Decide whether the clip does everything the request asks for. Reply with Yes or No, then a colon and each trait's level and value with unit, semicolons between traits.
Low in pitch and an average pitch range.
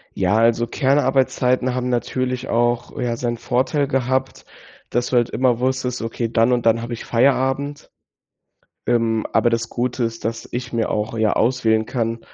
No: low, 120 Hz; narrow, 1.9 semitones